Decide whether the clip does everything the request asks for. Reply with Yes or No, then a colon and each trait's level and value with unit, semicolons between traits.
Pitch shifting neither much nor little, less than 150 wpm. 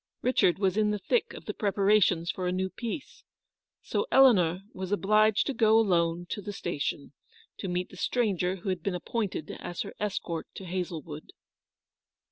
No: average, 3.2 semitones; average, 175 wpm